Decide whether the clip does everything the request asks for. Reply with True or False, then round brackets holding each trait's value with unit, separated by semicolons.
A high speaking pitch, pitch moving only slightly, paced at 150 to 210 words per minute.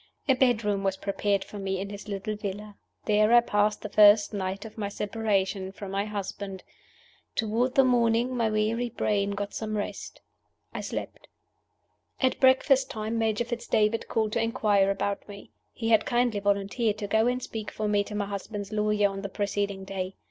True (210 Hz; 2.0 semitones; 185 wpm)